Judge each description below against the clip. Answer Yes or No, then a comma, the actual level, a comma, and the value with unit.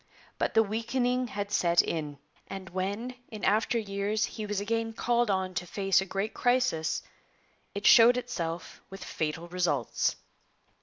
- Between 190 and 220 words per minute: No, average, 150 wpm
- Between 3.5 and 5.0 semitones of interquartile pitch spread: Yes, average, 3.9 semitones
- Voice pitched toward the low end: No, high, 200 Hz